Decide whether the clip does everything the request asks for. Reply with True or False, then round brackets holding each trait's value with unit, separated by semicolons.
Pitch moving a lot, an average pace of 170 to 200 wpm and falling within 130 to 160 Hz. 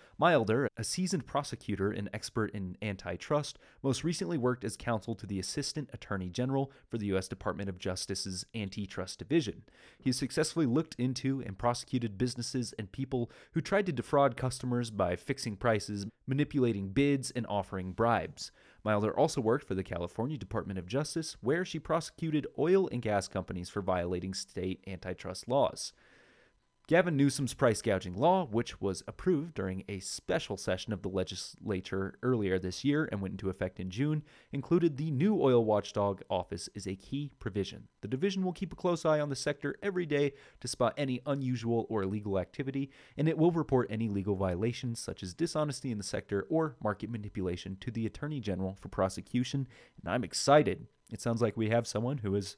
False (6.1 semitones; 175 wpm; 120 Hz)